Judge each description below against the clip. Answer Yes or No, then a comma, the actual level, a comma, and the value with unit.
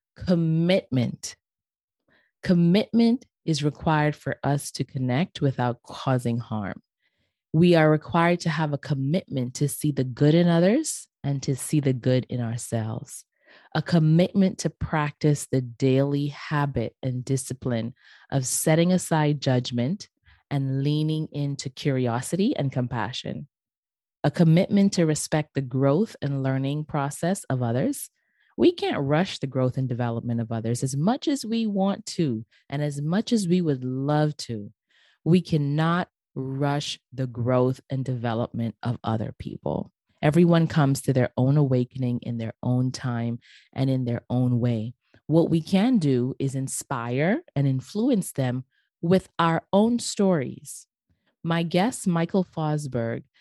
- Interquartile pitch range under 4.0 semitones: No, average, 4.8 semitones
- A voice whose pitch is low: No, medium, 145 Hz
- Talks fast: No, average, 140 wpm